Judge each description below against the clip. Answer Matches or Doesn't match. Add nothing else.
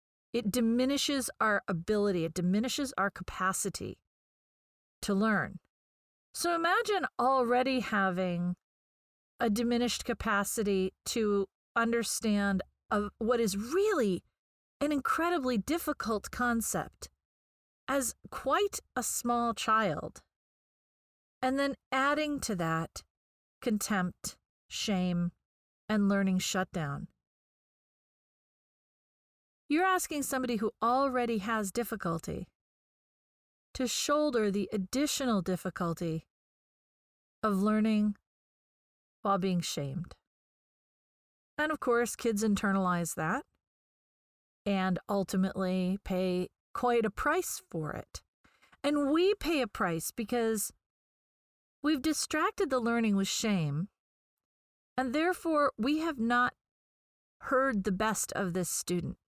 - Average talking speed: Doesn't match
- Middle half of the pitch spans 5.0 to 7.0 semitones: Matches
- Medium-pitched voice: Doesn't match